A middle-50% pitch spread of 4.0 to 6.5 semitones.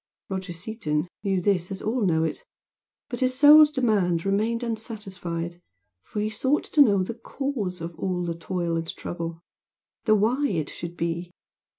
Yes: average, 5.0 semitones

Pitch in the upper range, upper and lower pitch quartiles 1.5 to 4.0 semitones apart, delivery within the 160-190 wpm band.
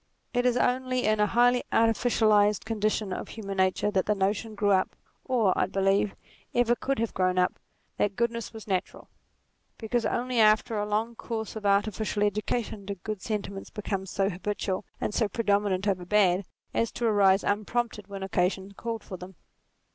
Yes: high, 210 Hz; average, 2.7 semitones; average, 170 wpm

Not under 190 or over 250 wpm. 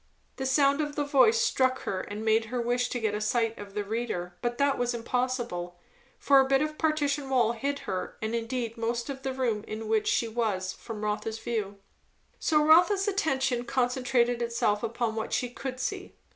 Yes: average, 195 wpm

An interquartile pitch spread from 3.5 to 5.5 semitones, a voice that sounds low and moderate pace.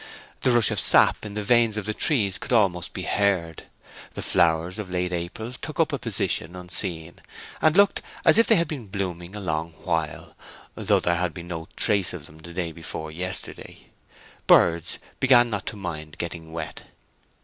Yes: average, 4.2 semitones; very low, 90 Hz; average, 185 wpm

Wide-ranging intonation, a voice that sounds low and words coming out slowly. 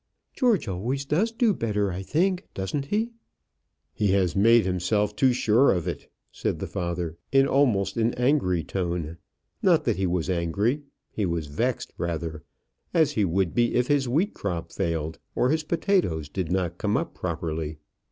No: wide, 7.9 semitones; low, 100 Hz; average, 170 wpm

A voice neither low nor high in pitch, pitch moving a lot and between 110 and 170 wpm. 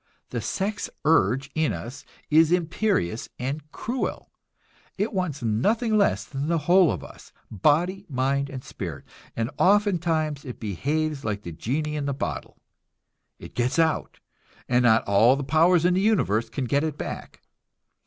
Yes: medium, 150 Hz; wide, 5.7 semitones; average, 155 wpm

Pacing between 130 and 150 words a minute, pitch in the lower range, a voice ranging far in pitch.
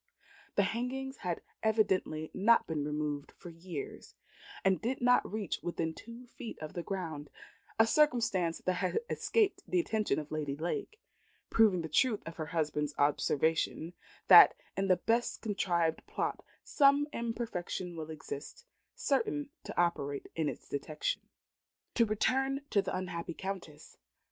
No: average, 145 wpm; medium, 185 Hz; wide, 6.5 semitones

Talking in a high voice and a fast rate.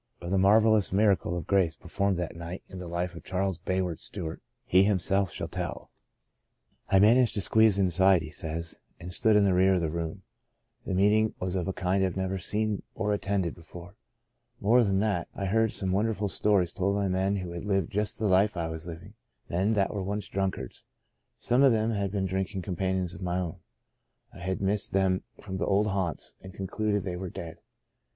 No: very low, 95 Hz; fast, 210 wpm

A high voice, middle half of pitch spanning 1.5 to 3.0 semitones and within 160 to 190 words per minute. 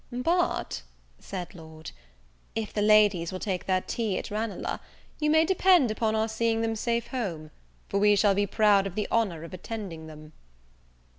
No: high, 210 Hz; average, 3.7 semitones; average, 170 wpm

